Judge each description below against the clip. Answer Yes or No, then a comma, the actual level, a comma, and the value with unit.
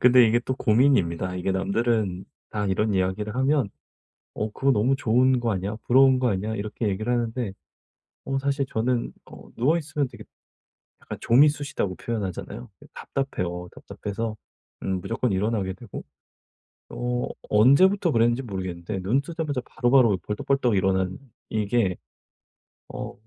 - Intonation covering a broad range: No, average, 5.0 semitones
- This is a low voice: Yes, low, 115 Hz